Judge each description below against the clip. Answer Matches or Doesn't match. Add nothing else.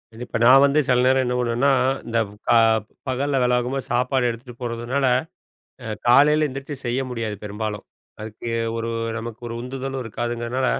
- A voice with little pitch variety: Matches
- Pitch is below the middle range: Matches